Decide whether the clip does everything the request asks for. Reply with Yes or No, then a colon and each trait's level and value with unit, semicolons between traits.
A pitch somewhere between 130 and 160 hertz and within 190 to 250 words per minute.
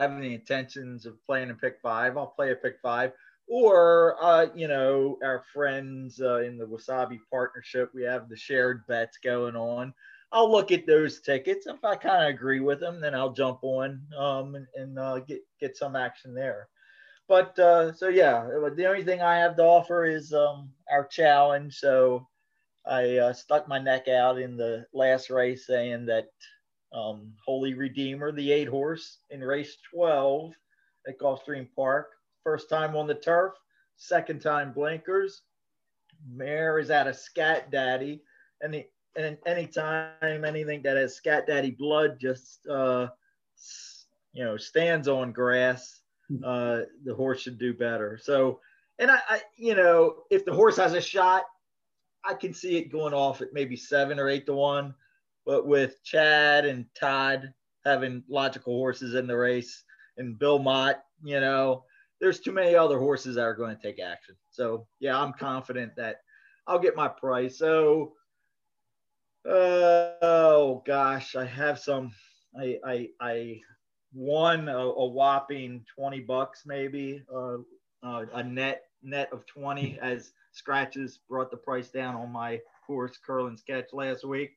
No: low, 135 Hz; average, 165 wpm